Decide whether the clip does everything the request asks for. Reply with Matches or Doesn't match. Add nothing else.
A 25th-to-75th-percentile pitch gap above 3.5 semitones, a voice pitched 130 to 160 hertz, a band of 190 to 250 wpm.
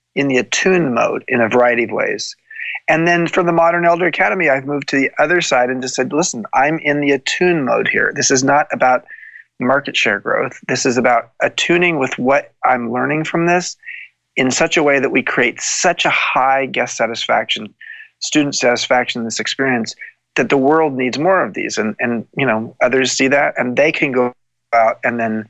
Matches